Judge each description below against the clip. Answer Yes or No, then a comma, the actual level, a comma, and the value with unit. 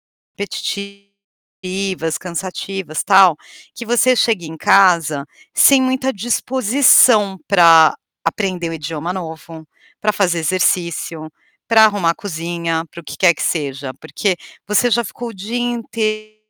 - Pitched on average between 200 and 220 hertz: No, high, 190 Hz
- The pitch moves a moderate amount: Yes, average, 4.5 semitones